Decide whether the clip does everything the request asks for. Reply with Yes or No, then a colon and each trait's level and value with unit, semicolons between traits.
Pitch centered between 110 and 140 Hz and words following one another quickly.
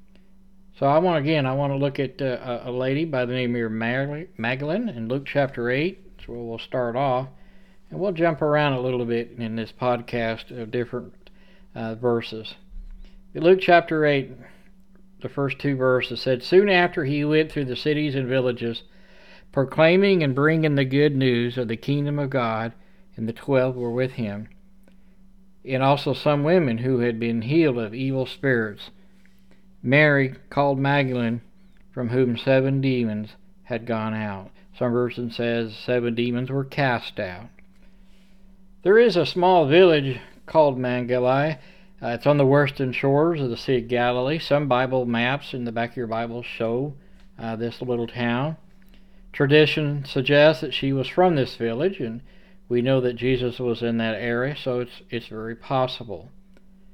No: low, 135 Hz; average, 165 wpm